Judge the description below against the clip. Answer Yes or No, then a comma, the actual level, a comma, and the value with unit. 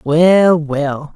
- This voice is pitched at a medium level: Yes, medium, 160 Hz